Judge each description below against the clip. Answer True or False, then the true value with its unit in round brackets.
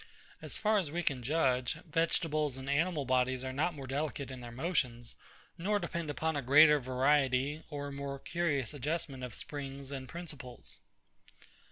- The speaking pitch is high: False (140 Hz)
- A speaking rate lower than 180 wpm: True (160 wpm)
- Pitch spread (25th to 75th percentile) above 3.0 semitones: True (3.5 semitones)